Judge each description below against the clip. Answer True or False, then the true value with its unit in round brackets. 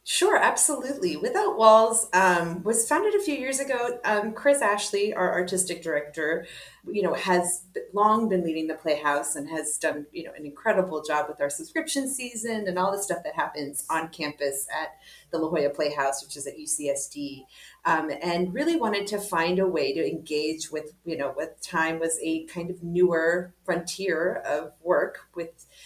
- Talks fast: False (180 wpm)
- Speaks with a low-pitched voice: False (175 Hz)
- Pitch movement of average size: False (5.7 semitones)